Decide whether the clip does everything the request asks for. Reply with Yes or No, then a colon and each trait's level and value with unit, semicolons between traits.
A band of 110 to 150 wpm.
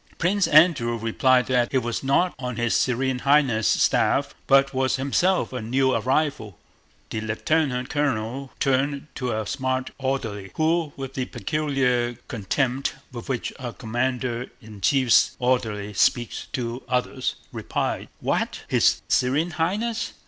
Yes: slow, 135 wpm